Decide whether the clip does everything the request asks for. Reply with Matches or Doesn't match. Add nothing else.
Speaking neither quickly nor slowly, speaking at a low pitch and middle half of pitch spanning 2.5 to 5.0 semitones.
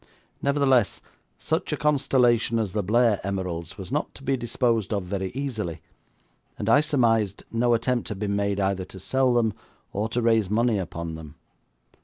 Matches